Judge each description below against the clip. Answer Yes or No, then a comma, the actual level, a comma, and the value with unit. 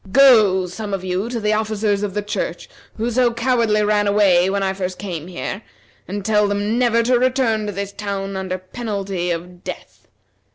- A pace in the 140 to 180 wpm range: No, average, 190 wpm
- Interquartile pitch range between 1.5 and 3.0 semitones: Yes, narrow, 2.6 semitones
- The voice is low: No, high, 205 Hz